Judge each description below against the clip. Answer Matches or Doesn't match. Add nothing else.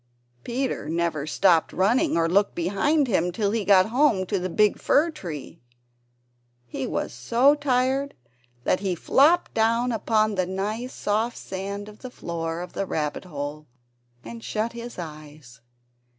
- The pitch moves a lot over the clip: Matches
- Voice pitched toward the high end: Matches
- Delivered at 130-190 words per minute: Matches